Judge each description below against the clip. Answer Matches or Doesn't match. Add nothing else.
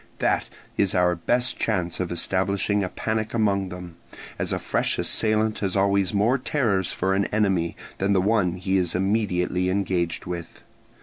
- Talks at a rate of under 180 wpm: Matches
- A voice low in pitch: Matches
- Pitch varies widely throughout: Doesn't match